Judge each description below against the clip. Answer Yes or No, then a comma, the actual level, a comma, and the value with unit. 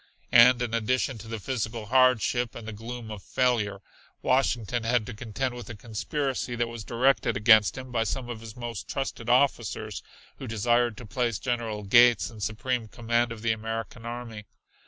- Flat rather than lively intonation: Yes, narrow, 2.0 semitones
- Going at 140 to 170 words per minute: No, average, 180 wpm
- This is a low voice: Yes, low, 115 Hz